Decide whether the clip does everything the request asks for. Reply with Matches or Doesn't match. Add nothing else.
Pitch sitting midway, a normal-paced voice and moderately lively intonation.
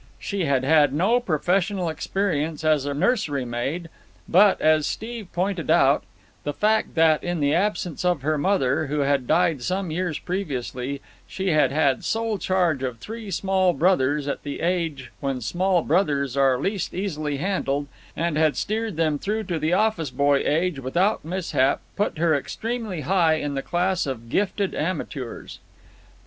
Matches